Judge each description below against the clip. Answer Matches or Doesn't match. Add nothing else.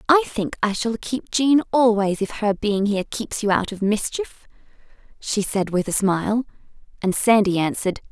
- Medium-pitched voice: Doesn't match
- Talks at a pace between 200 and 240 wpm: Doesn't match